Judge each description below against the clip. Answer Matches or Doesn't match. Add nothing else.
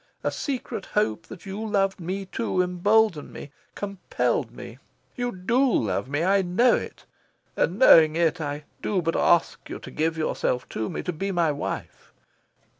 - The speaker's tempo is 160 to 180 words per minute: Matches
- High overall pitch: Doesn't match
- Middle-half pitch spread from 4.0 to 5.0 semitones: Matches